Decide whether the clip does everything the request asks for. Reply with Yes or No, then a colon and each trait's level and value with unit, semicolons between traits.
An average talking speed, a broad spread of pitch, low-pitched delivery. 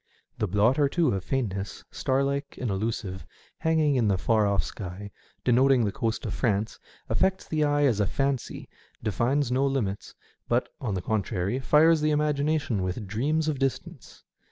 Yes: average, 180 wpm; wide, 5.7 semitones; low, 125 Hz